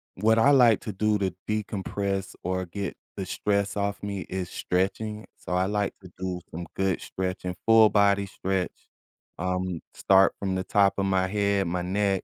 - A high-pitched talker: No, very low, 95 Hz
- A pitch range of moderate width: No, narrow, 1.8 semitones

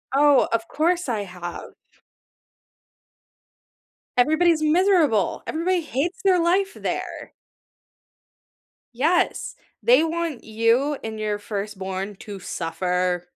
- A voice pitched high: Yes, very high, 260 Hz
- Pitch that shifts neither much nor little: No, wide, 8.7 semitones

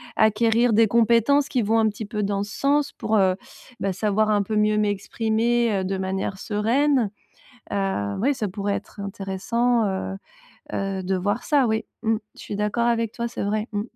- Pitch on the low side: No, high, 215 Hz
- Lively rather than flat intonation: No, average, 2.8 semitones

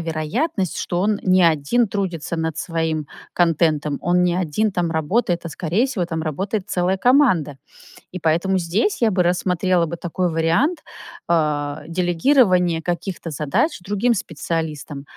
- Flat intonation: No, average, 3.0 semitones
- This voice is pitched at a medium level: Yes, medium, 175 Hz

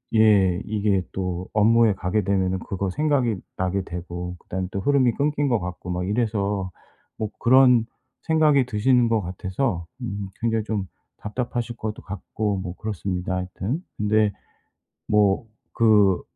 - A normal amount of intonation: Yes, average, 3.8 semitones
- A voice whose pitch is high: No, low, 105 Hz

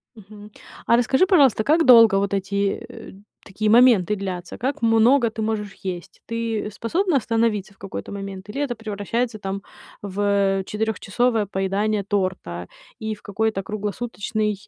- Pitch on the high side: Yes, high, 210 Hz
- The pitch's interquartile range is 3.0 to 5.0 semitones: No, narrow, 2.6 semitones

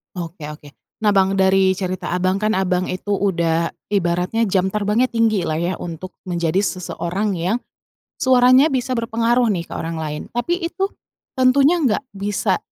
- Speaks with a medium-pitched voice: No, high, 195 Hz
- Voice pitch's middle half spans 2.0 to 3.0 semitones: No, average, 4.5 semitones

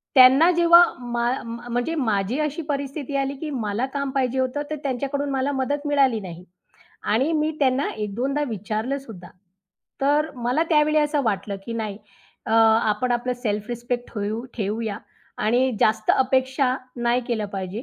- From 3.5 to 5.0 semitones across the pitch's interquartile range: Yes, average, 4.0 semitones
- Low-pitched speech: No, very high, 250 Hz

